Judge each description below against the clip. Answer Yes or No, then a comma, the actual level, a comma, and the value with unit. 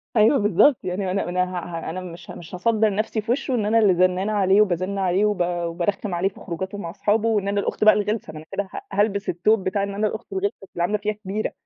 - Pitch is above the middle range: Yes, high, 200 Hz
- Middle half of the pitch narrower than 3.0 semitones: Yes, narrow, 2.6 semitones